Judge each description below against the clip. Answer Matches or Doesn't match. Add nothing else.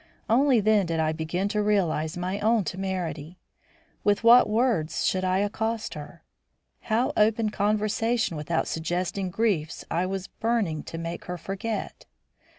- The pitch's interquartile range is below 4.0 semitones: Doesn't match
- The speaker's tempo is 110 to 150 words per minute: Matches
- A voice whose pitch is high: Matches